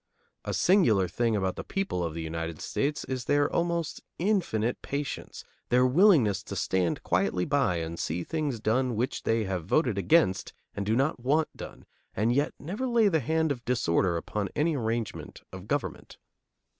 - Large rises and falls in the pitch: Yes, wide, 8.1 semitones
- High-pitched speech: No, low, 120 Hz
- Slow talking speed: No, average, 170 wpm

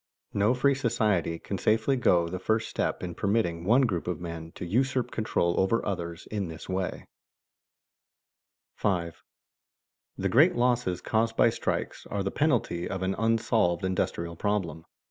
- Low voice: Yes, low, 100 Hz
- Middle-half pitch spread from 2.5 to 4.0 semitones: No, average, 4.8 semitones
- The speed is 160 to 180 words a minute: Yes, average, 165 wpm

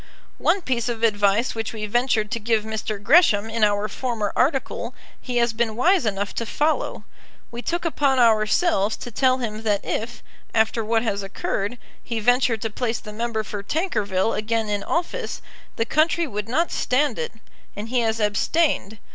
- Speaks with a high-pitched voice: Yes, high, 230 Hz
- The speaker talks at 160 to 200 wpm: Yes, average, 175 wpm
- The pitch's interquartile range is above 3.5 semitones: No, average, 3.2 semitones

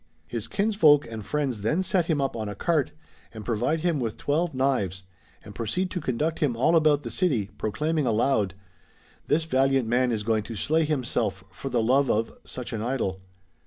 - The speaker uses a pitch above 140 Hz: No, low, 130 Hz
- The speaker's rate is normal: Yes, average, 195 wpm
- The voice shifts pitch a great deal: Yes, wide, 5.7 semitones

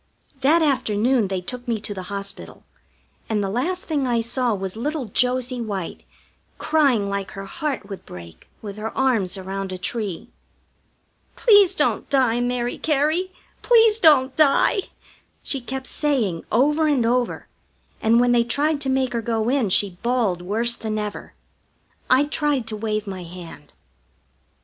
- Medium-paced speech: Yes, average, 155 wpm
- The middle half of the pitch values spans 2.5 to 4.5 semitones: No, average, 5.2 semitones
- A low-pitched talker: No, high, 240 Hz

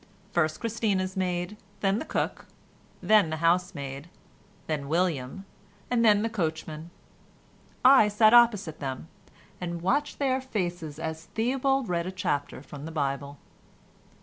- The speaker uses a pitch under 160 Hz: No, medium, 180 Hz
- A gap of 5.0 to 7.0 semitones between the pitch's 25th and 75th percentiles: Yes, wide, 5.5 semitones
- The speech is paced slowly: Yes, slow, 130 wpm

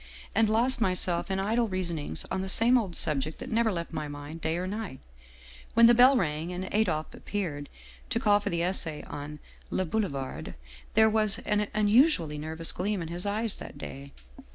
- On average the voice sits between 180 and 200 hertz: Yes, medium, 185 Hz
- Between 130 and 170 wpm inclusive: No, average, 190 wpm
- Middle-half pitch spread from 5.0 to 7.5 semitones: Yes, wide, 5.5 semitones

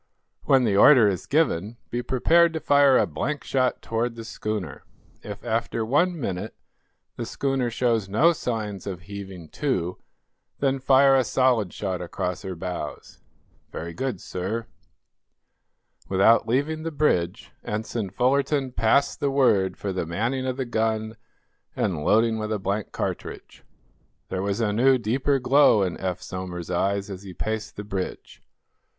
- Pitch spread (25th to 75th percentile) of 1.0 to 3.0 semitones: No, wide, 5.4 semitones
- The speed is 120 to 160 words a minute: Yes, average, 155 wpm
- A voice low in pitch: Yes, low, 110 Hz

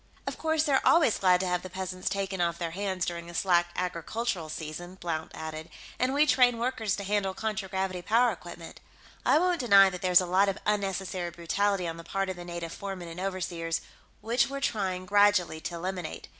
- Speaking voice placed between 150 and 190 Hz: Yes, medium, 185 Hz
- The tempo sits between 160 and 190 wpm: No, average, 200 wpm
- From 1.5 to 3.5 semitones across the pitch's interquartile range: Yes, average, 2.9 semitones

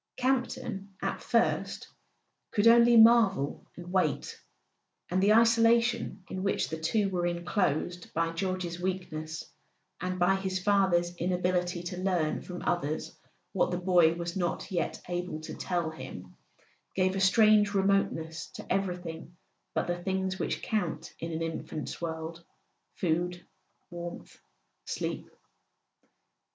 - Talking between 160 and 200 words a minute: No, slow, 135 wpm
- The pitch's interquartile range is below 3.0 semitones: Yes, narrow, 2.4 semitones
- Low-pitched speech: No, medium, 180 Hz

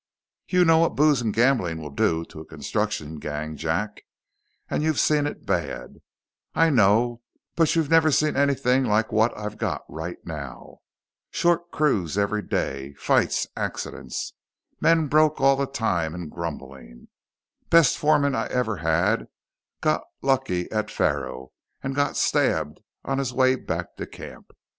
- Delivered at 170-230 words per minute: No, average, 150 wpm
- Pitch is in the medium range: No, low, 115 Hz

